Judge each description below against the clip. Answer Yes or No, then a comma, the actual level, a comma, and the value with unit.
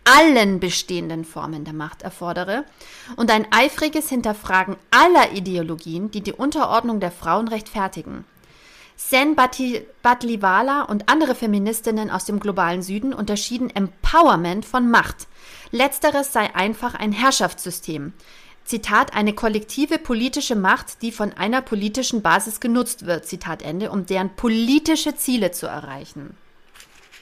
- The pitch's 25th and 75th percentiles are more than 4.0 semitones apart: Yes, average, 5.2 semitones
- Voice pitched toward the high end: Yes, high, 215 Hz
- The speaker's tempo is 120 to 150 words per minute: Yes, slow, 125 wpm